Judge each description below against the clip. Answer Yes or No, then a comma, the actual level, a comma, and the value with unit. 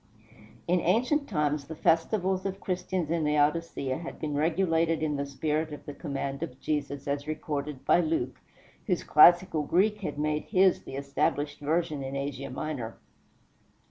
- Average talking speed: Yes, average, 155 wpm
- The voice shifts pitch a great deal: No, average, 3.3 semitones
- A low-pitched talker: No, medium, 155 Hz